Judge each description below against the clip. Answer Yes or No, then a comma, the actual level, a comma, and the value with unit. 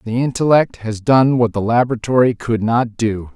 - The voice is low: Yes, low, 115 Hz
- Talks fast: No, average, 180 wpm